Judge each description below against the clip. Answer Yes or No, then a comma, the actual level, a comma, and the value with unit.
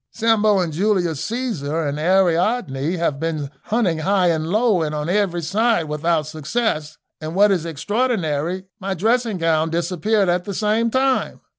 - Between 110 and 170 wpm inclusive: Yes, average, 155 wpm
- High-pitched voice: No, medium, 180 Hz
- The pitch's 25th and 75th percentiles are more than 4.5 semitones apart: Yes, average, 5.2 semitones